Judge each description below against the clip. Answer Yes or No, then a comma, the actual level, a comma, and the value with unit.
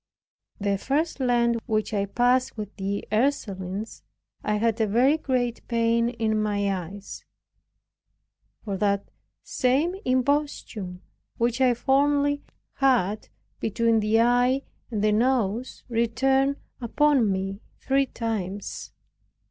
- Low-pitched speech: No, high, 230 Hz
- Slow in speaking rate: Yes, slow, 115 wpm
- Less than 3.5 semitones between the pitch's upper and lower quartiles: No, average, 3.8 semitones